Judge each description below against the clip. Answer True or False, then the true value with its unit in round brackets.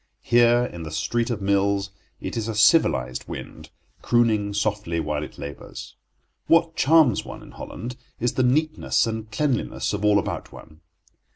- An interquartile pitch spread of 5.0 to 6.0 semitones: False (3.9 semitones)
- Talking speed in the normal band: True (160 wpm)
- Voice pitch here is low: True (110 Hz)